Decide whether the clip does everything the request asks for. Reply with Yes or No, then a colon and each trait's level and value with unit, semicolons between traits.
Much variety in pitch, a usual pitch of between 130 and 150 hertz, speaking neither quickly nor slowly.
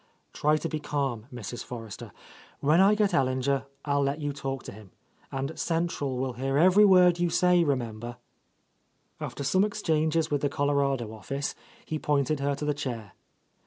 No: average, 3.6 semitones; medium, 140 Hz; average, 180 wpm